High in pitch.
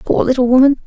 Yes: very high, 255 Hz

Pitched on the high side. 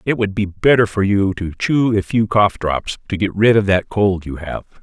No: low, 100 Hz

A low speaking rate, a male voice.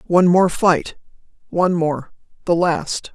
No: slow, 115 wpm; female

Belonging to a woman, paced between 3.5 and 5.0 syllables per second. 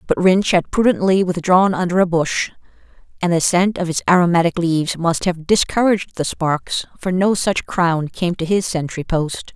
Yes: female; 4.8 syllables/s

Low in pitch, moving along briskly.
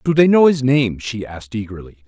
Yes: low, 120 Hz; fast, 230 wpm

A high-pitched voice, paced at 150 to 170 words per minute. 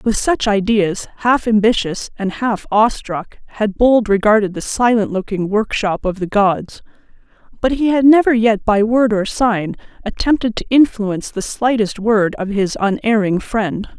Yes: high, 215 Hz; average, 165 wpm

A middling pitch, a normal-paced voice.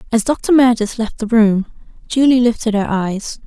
No: high, 230 Hz; average, 175 wpm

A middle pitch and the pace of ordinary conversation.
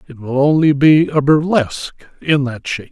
Yes: medium, 145 Hz; average, 185 wpm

